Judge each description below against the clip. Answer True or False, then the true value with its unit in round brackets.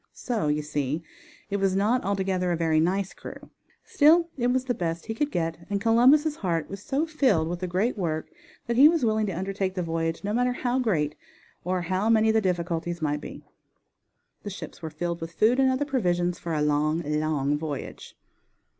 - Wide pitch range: True (6.1 semitones)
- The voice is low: False (185 Hz)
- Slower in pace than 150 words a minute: False (200 wpm)